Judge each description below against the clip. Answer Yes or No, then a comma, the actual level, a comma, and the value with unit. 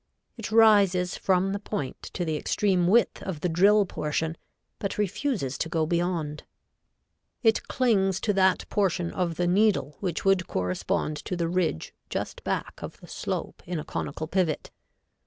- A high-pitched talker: No, medium, 180 Hz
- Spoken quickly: No, average, 160 wpm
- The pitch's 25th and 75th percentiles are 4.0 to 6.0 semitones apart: No, average, 3.6 semitones